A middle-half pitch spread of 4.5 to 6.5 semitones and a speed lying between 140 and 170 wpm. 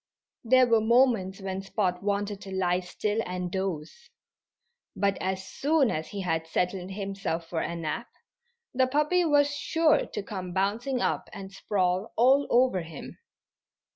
Yes: average, 5.1 semitones; average, 150 wpm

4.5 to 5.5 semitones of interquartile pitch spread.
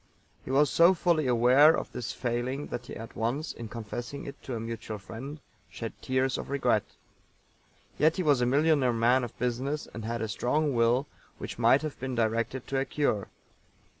No: average, 3.4 semitones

